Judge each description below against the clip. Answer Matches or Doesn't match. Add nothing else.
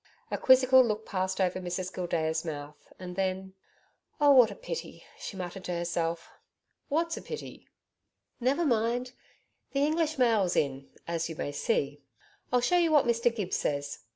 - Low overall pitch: Doesn't match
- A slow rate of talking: Doesn't match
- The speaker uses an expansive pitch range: Matches